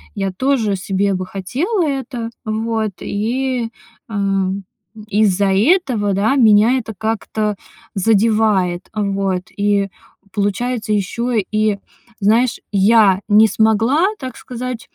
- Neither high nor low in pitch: No, high, 215 Hz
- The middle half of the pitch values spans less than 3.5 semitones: Yes, average, 3.1 semitones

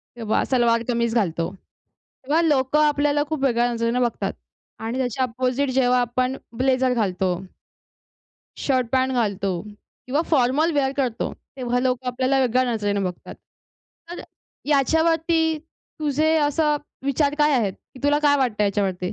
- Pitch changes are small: No, average, 3.7 semitones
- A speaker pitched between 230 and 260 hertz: Yes, very high, 255 Hz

